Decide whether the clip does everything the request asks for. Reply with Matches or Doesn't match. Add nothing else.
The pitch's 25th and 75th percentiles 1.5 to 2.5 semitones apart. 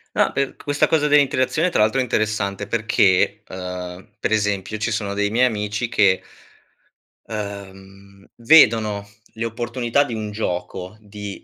Doesn't match